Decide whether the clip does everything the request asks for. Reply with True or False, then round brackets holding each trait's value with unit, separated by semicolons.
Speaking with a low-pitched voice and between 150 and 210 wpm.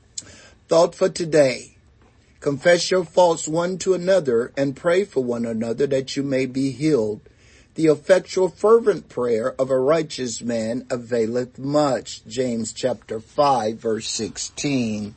False (130 Hz; 135 wpm)